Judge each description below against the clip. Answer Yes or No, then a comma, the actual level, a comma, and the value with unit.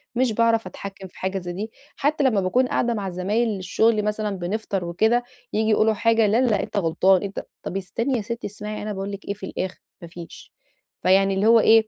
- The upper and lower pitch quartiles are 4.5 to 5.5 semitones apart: No, average, 2.9 semitones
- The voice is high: Yes, high, 210 Hz